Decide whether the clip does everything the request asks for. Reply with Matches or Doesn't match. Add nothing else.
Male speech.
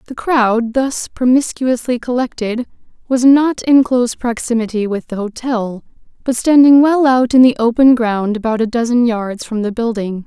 Doesn't match